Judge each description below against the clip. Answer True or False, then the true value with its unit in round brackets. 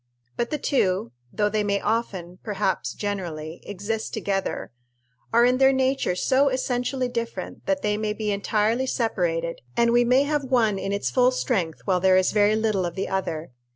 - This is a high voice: True (215 Hz)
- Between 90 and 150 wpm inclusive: False (180 wpm)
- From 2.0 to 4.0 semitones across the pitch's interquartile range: False (4.6 semitones)